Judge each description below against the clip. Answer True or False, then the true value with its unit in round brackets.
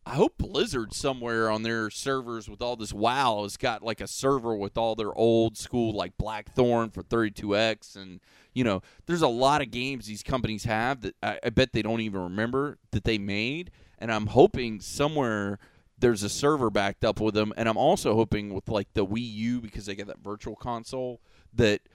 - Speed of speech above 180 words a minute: True (200 wpm)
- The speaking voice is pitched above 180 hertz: False (115 Hz)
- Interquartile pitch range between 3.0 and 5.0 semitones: False (2.6 semitones)